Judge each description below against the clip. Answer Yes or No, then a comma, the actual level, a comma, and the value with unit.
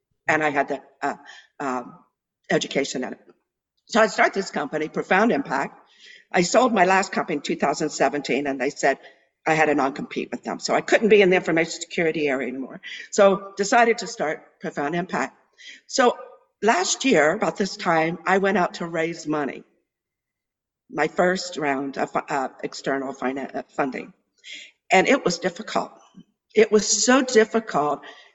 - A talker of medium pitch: Yes, medium, 180 Hz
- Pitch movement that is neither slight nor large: No, wide, 6.0 semitones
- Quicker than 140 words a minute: Yes, average, 160 wpm